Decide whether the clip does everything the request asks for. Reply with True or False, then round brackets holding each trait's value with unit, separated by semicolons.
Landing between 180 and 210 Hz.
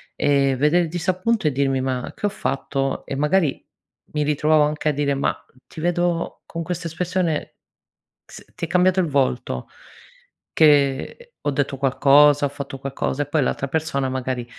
False (145 Hz)